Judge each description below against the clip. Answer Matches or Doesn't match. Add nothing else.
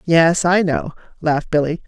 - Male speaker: Doesn't match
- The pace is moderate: Matches